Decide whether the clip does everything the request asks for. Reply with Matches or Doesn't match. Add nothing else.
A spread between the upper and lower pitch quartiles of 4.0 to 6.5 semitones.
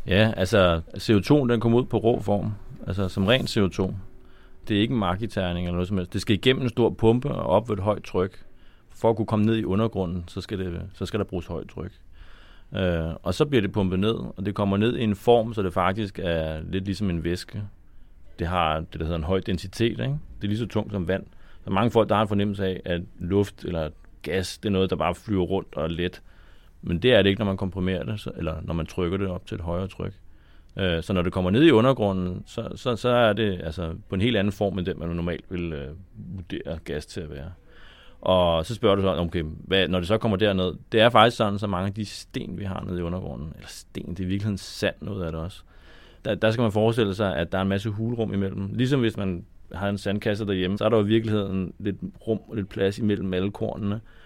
Doesn't match